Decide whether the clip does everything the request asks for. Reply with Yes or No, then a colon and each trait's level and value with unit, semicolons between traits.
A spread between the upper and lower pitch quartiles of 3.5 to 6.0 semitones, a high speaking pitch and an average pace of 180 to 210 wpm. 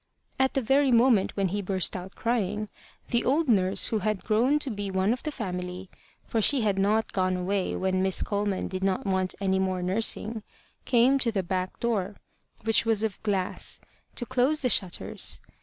Yes: average, 3.8 semitones; high, 205 Hz; average, 190 wpm